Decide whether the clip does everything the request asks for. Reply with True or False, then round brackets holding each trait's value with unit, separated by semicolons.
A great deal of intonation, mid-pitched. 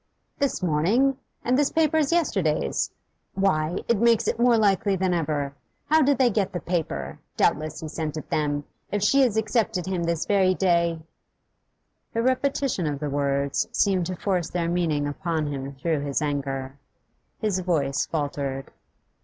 True (6.2 semitones; 175 Hz)